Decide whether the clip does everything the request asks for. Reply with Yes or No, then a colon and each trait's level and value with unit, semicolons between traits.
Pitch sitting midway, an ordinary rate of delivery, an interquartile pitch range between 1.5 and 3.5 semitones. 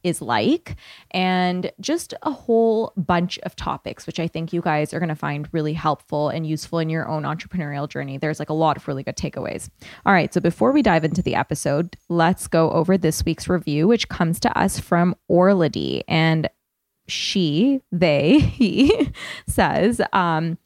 Yes: medium, 170 Hz; average, 180 wpm; average, 3.0 semitones